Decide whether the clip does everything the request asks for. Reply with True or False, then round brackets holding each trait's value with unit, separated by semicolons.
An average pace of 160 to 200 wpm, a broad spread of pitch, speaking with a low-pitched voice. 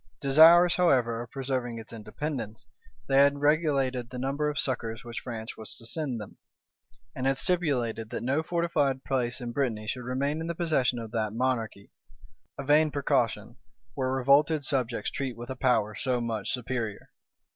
False (165 wpm; 3.5 semitones; 130 Hz)